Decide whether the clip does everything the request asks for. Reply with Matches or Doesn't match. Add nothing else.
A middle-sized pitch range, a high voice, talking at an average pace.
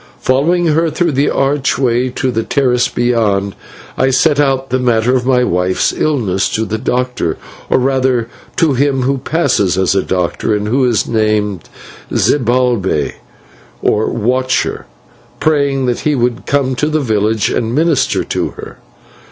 Doesn't match